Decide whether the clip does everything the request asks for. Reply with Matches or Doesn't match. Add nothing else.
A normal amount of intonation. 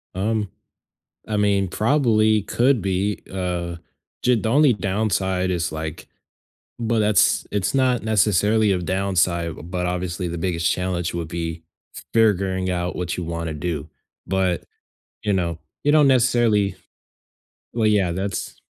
Matches